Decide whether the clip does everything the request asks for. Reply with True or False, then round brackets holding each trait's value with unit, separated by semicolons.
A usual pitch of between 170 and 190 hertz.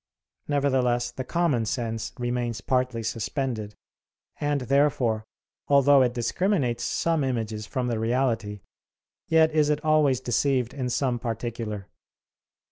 False (125 Hz)